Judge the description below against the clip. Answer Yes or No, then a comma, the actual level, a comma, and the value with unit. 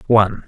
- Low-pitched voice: Yes, low, 110 Hz